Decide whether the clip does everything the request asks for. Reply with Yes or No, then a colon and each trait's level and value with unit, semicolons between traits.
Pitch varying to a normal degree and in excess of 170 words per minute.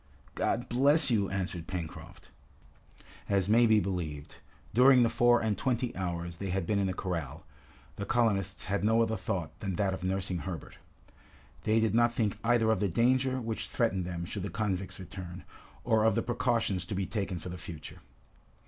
Yes: average, 4.0 semitones; average, 185 wpm